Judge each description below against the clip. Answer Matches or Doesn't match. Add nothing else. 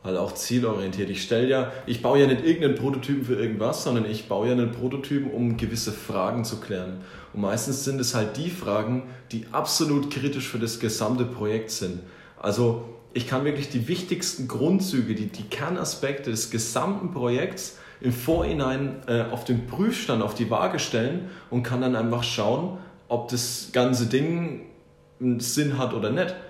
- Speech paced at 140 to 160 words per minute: Doesn't match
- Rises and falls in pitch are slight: Doesn't match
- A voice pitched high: Doesn't match